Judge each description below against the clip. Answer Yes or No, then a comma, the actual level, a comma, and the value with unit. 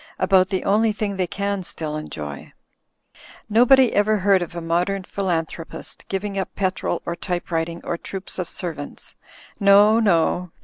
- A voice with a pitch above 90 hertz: Yes, medium, 185 Hz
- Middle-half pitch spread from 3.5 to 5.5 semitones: No, average, 3.1 semitones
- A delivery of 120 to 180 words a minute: Yes, average, 150 wpm